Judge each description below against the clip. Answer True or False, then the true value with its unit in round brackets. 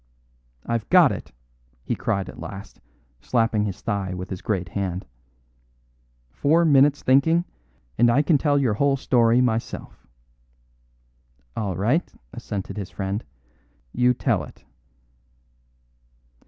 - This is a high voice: False (115 Hz)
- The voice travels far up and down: True (5.9 semitones)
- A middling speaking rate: False (120 wpm)